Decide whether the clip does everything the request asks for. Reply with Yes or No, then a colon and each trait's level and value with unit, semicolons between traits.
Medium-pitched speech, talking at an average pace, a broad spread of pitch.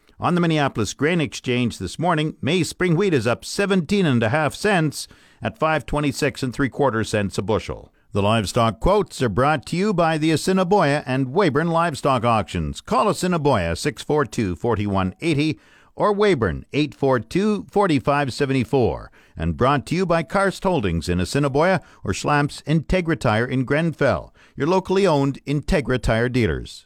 Yes: medium, 145 Hz; average, 145 wpm; wide, 5.9 semitones